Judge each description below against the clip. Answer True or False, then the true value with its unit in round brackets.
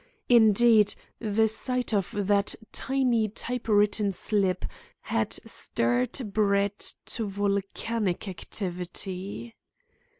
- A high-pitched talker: True (205 Hz)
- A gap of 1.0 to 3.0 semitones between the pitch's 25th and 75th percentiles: True (2.4 semitones)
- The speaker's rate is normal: False (90 wpm)